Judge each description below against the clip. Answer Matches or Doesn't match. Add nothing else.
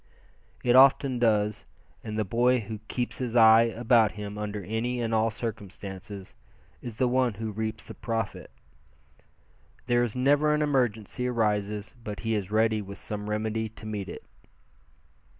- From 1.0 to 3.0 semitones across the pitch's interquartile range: Matches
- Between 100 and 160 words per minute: Matches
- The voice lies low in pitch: Matches